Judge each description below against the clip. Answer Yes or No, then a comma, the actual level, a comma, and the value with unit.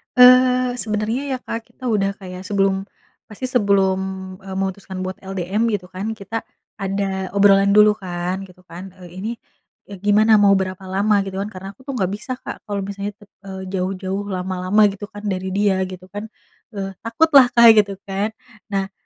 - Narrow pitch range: Yes, narrow, 1.9 semitones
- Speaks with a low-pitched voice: No, high, 200 Hz